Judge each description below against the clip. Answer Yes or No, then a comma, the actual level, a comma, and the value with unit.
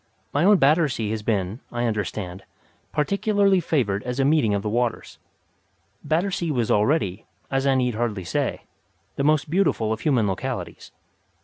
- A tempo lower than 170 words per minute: Yes, average, 150 wpm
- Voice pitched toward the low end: Yes, low, 125 Hz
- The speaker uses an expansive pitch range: Yes, wide, 6.4 semitones